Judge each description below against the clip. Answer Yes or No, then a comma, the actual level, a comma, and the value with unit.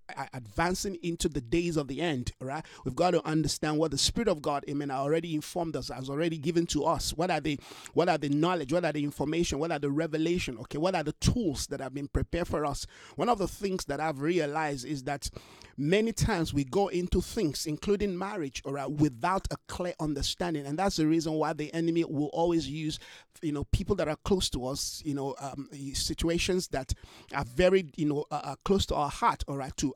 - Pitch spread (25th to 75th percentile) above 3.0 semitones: Yes, average, 3.4 semitones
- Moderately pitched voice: Yes, medium, 155 Hz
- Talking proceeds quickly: Yes, fast, 225 wpm